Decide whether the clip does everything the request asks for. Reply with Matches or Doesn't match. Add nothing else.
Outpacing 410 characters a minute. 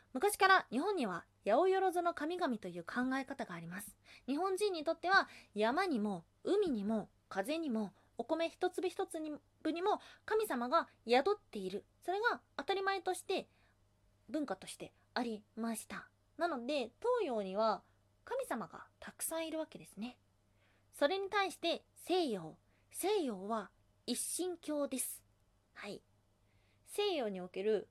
Doesn't match